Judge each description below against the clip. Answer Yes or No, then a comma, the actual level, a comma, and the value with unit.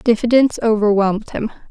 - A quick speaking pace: No, slow, 105 wpm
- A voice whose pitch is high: Yes, high, 220 Hz